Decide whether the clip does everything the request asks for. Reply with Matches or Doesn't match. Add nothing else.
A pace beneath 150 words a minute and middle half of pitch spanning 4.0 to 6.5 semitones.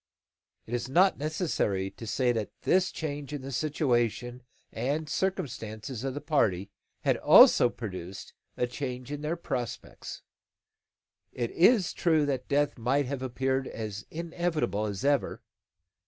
Matches